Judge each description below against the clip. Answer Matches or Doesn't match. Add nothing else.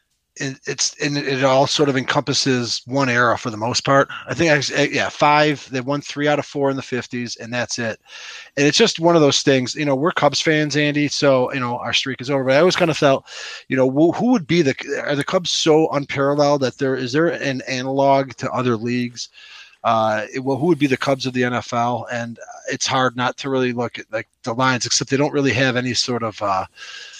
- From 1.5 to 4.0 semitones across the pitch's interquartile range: Matches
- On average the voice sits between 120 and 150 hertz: Matches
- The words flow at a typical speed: Doesn't match